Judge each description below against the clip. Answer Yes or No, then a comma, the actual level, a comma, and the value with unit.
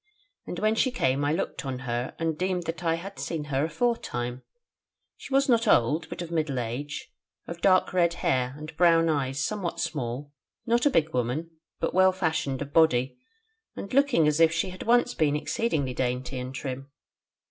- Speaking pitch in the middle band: Yes, medium, 160 Hz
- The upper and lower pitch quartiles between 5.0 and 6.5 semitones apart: Yes, wide, 5.5 semitones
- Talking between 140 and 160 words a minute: No, average, 185 wpm